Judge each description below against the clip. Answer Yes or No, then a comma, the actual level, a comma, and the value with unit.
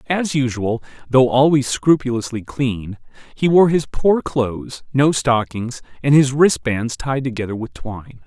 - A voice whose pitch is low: Yes, low, 130 Hz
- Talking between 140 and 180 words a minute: Yes, average, 145 wpm